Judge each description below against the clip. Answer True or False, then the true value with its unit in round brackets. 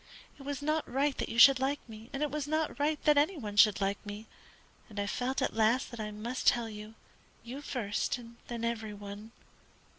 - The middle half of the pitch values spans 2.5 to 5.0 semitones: True (4.7 semitones)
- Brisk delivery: True (210 wpm)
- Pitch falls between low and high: False (235 Hz)